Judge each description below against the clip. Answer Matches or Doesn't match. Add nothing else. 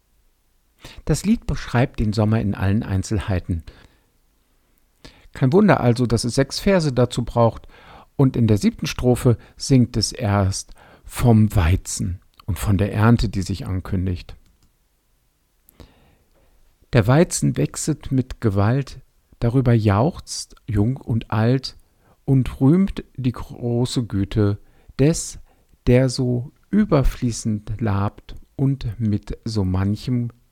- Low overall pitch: Matches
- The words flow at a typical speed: Doesn't match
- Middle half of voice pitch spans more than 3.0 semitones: Matches